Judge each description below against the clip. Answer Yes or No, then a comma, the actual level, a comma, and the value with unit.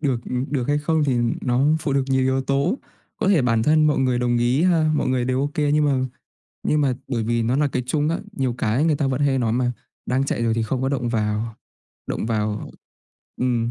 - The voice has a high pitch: No, low, 130 Hz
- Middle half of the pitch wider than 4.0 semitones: No, average, 3.4 semitones